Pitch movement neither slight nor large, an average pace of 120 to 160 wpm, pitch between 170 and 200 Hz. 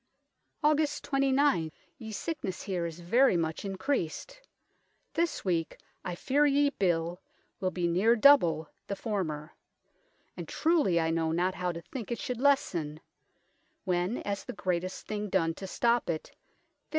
No: wide, 7.8 semitones; average, 150 wpm; high, 190 Hz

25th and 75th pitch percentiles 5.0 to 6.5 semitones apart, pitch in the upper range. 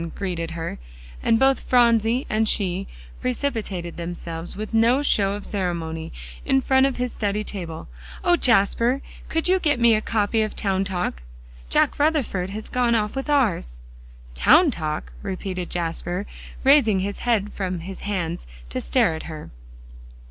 Yes: wide, 5.5 semitones; high, 205 Hz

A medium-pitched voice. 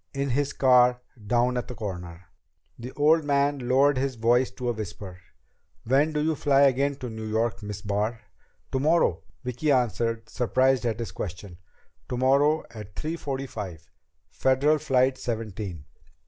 No: low, 125 Hz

